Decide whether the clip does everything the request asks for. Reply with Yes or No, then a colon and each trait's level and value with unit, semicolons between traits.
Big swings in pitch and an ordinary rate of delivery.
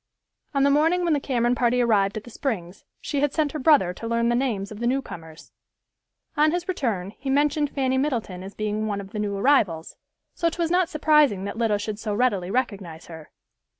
No: wide, 6.2 semitones; fast, 210 wpm